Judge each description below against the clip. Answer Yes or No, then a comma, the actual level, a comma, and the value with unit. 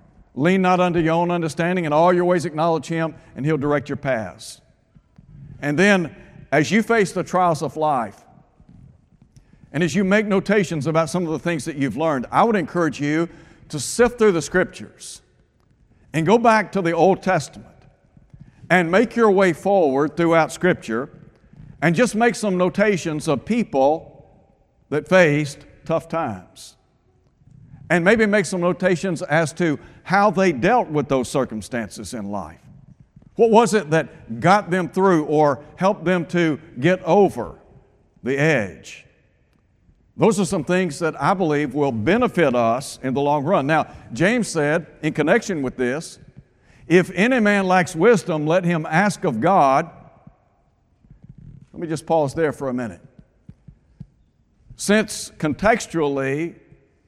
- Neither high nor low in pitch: Yes, medium, 165 Hz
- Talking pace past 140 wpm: Yes, average, 150 wpm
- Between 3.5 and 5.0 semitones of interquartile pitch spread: Yes, average, 4.2 semitones